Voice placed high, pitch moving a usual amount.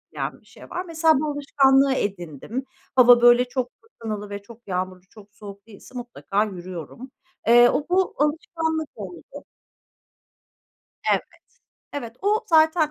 No: high, 245 Hz; wide, 6.7 semitones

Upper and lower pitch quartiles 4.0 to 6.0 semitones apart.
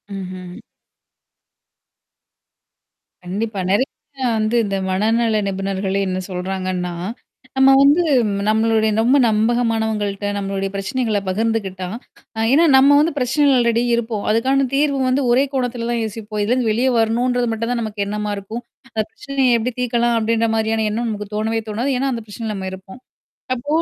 No: average, 3.2 semitones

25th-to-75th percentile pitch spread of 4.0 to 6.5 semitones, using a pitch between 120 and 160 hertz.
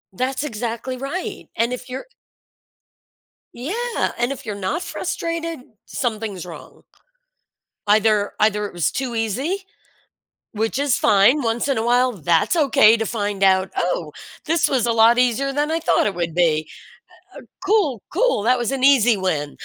No: average, 5.0 semitones; high, 235 Hz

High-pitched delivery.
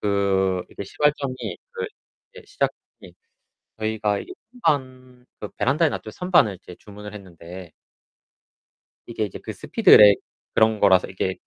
No: low, 105 Hz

